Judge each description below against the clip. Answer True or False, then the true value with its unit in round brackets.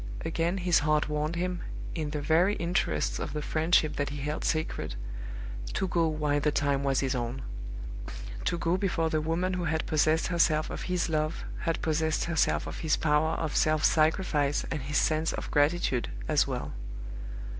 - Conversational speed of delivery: True (175 wpm)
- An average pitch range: False (2.2 semitones)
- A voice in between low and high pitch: True (155 Hz)